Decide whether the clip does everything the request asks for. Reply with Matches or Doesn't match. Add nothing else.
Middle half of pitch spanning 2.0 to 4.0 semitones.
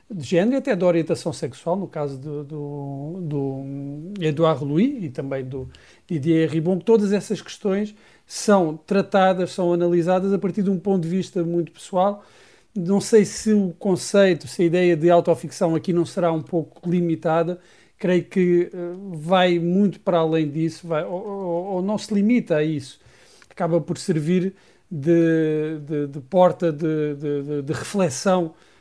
Matches